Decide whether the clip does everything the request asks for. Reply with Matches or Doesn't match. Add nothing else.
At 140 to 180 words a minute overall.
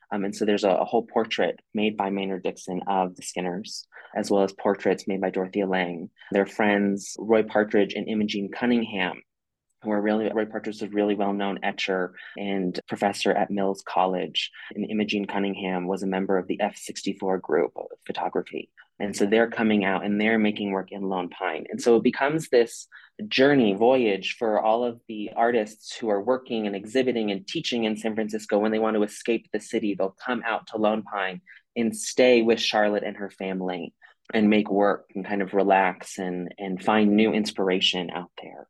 Doesn't match